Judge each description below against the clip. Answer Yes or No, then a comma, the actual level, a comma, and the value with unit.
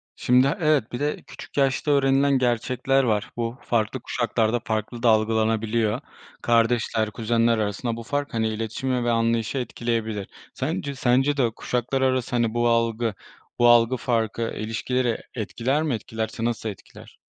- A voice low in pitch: Yes, low, 120 Hz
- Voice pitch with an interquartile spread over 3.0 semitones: No, narrow, 2.4 semitones